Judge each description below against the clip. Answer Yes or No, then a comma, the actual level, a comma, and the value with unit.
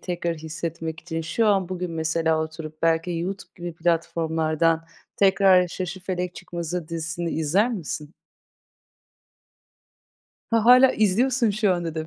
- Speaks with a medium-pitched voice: Yes, medium, 170 Hz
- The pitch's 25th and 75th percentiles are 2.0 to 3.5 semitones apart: Yes, average, 2.7 semitones